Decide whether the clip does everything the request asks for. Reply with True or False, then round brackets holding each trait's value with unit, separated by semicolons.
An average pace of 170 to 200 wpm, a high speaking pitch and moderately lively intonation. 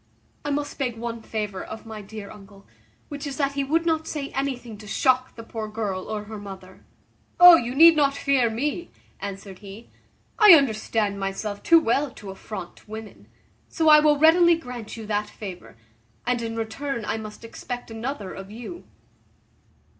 True (175 wpm; 230 Hz; 5.0 semitones)